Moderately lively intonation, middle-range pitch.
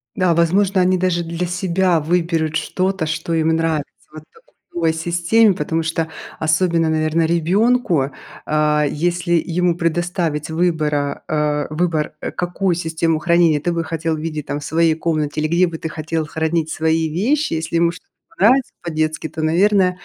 No: narrow, 1.9 semitones; medium, 165 Hz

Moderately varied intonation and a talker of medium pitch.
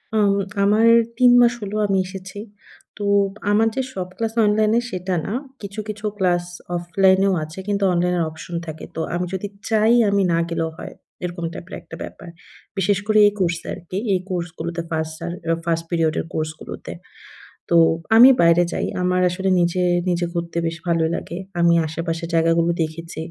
Yes: average, 3.0 semitones; medium, 180 Hz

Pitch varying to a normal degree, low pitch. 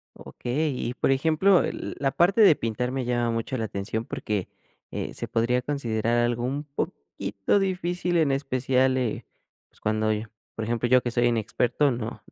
Yes: average, 3.8 semitones; low, 125 Hz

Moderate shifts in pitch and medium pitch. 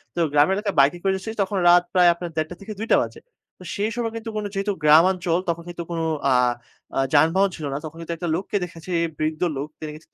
Yes: average, 3.7 semitones; medium, 175 Hz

